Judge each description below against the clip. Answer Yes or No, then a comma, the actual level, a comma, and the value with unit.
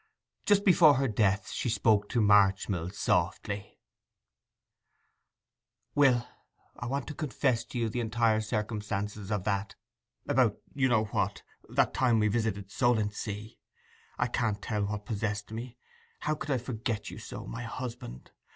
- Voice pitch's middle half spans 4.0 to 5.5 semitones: No, average, 3.1 semitones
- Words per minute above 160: No, slow, 135 wpm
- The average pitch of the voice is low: Yes, low, 110 Hz